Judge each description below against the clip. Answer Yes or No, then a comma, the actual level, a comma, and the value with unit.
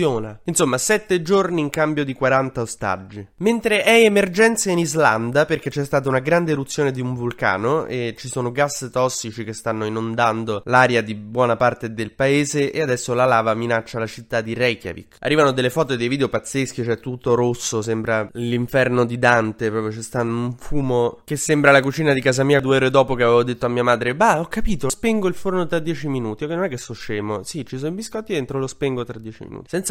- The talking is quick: Yes, fast, 215 wpm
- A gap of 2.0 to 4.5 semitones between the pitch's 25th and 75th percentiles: Yes, average, 4.2 semitones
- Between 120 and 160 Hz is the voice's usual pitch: Yes, low, 130 Hz